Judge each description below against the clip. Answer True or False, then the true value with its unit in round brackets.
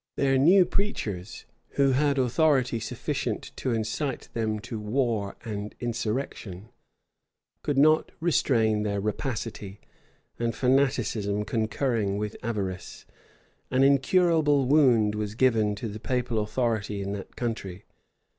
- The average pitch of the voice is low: True (115 Hz)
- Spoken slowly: True (120 wpm)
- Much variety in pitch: False (4.3 semitones)